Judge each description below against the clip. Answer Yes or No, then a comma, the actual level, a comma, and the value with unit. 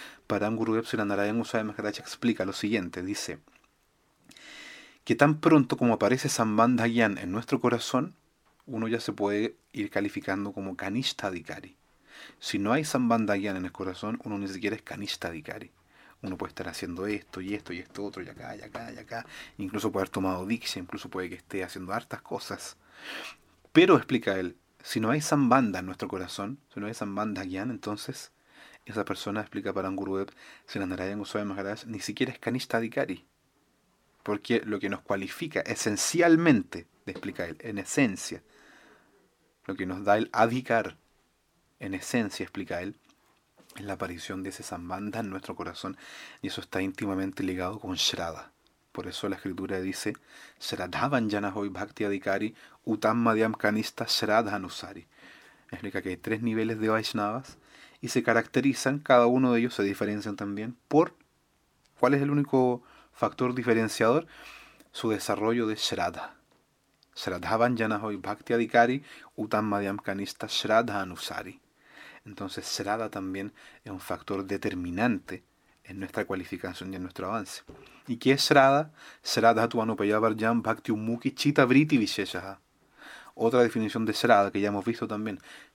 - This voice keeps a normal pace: Yes, average, 150 wpm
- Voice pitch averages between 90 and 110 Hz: Yes, low, 105 Hz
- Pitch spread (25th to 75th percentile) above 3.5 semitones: No, average, 3.0 semitones